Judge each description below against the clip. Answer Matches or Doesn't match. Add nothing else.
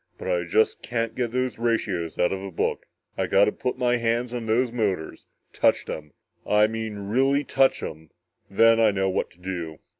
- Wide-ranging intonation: Doesn't match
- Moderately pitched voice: Doesn't match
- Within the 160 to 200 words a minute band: Matches